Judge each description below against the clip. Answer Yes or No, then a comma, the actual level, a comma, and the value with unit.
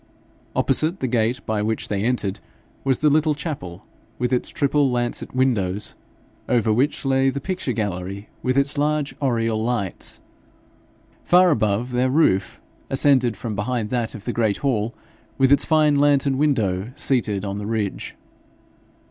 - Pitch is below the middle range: Yes, low, 125 Hz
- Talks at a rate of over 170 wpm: No, average, 150 wpm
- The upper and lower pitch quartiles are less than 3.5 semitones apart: No, average, 4.6 semitones